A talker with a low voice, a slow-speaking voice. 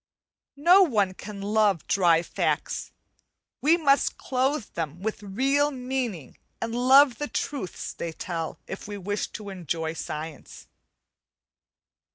No: high, 210 Hz; slow, 125 wpm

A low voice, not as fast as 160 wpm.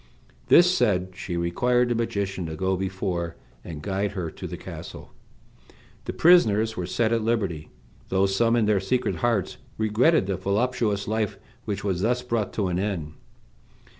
No: low, 100 Hz; average, 165 wpm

